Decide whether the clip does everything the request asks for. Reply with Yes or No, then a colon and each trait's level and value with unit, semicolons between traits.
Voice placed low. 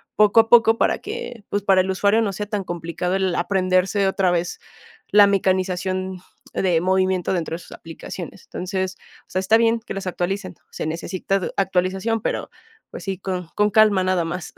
No: high, 190 Hz